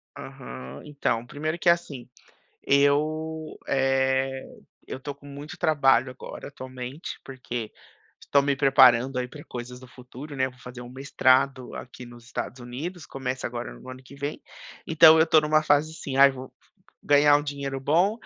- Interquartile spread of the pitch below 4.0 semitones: Yes, narrow, 2.5 semitones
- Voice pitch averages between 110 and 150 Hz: Yes, low, 135 Hz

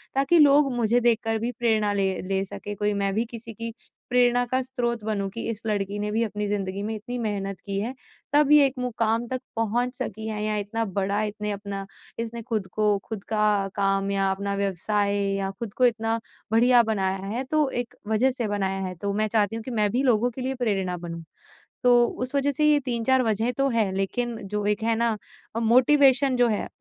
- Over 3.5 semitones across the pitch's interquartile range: No, average, 3.2 semitones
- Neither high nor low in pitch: No, high, 220 Hz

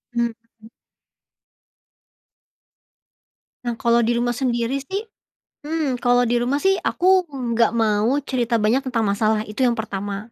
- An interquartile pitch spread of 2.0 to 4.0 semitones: Yes, average, 2.8 semitones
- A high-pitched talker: Yes, high, 240 Hz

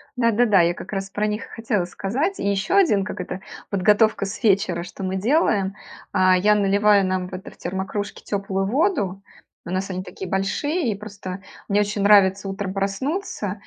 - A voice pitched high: Yes, high, 200 Hz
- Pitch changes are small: Yes, narrow, 1.9 semitones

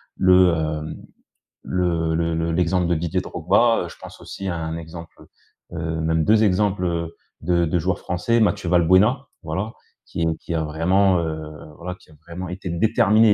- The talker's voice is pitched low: Yes, very low, 85 Hz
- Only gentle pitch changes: Yes, narrow, 2.3 semitones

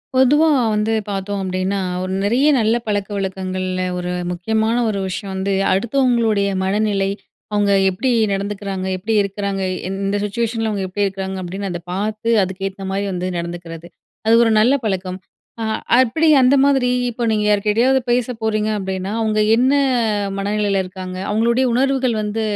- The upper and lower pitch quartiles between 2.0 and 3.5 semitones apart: Yes, average, 2.9 semitones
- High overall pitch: Yes, high, 205 Hz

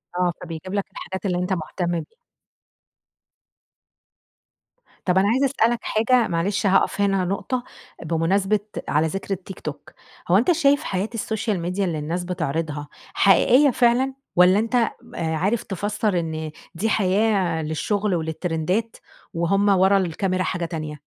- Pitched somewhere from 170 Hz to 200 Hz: Yes, high, 190 Hz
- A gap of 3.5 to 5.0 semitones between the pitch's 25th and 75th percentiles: Yes, average, 4.0 semitones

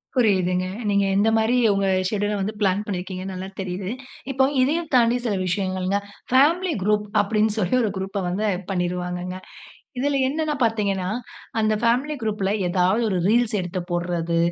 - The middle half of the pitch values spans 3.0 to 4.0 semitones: Yes, average, 3.5 semitones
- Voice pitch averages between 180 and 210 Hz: Yes, high, 200 Hz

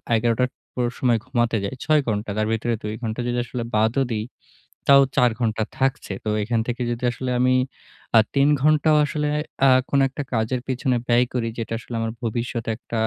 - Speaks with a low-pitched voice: Yes, low, 120 Hz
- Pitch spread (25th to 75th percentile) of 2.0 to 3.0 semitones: Yes, narrow, 2.4 semitones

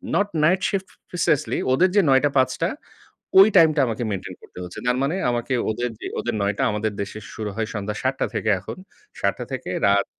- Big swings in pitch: Yes, wide, 6.6 semitones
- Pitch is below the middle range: Yes, low, 120 Hz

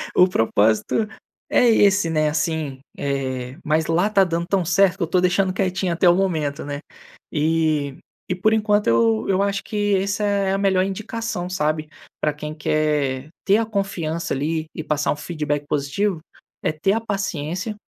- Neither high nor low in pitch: Yes, medium, 170 Hz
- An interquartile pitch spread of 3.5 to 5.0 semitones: Yes, average, 4.6 semitones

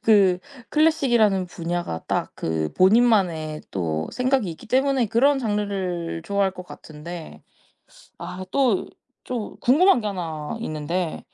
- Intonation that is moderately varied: No, wide, 6.1 semitones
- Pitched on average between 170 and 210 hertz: Yes, high, 190 Hz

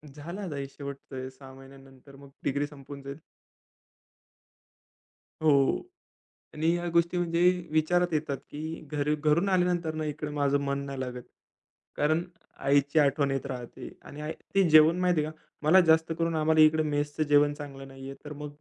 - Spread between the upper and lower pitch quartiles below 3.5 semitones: Yes, narrow, 2.5 semitones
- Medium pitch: Yes, medium, 150 Hz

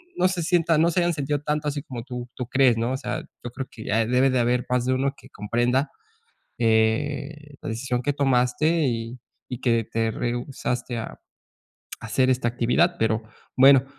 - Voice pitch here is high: No, low, 130 Hz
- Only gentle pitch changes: No, average, 3.3 semitones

